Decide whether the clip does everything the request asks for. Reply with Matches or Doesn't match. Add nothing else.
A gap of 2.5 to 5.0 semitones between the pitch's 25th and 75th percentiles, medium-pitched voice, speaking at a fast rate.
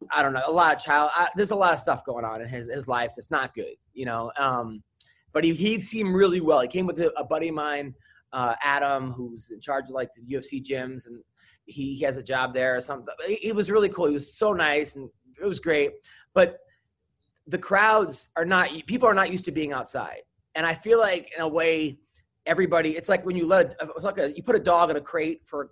Doesn't match